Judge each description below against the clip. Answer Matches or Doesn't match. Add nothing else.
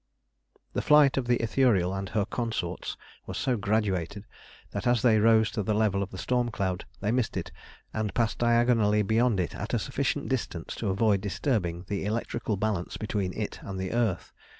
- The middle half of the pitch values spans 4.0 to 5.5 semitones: Doesn't match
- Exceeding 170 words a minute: Matches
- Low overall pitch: Matches